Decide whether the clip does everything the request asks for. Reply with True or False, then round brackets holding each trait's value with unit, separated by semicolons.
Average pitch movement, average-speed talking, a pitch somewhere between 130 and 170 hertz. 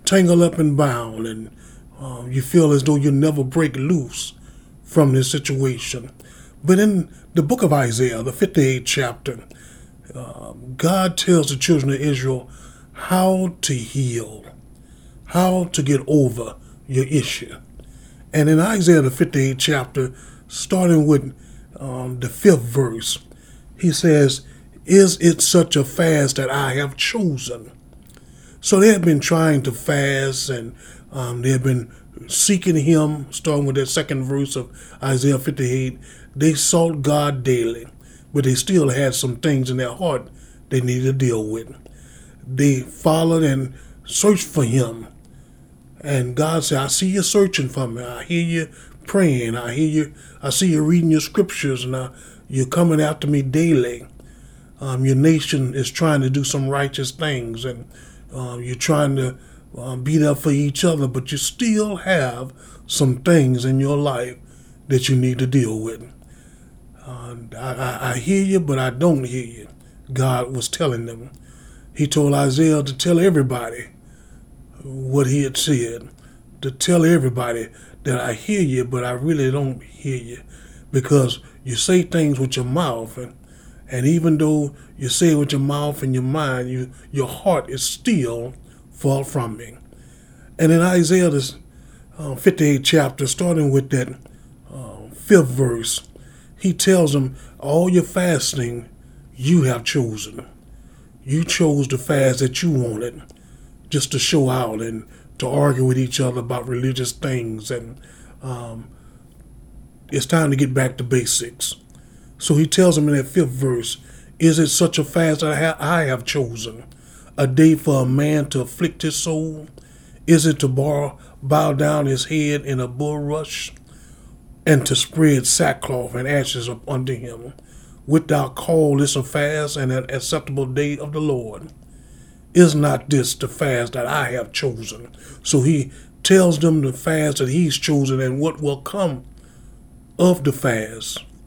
True (3.5 semitones; 160 wpm; 140 Hz)